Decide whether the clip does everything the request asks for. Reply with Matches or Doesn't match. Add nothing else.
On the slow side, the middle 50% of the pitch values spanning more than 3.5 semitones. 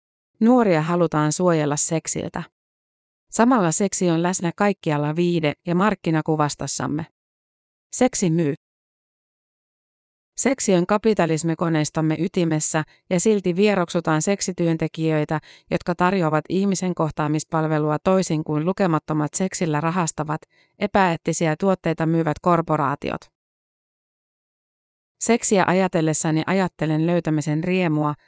Doesn't match